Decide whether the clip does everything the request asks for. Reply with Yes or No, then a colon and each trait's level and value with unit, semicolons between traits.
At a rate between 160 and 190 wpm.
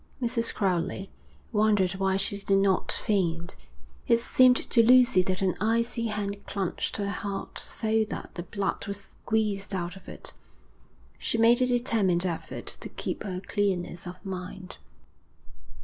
No: average, 150 wpm